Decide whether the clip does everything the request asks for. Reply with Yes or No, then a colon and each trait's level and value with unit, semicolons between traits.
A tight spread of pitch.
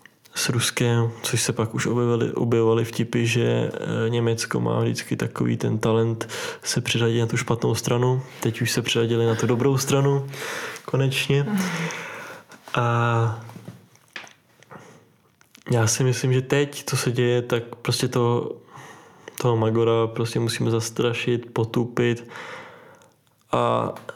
Yes: narrow, 2.3 semitones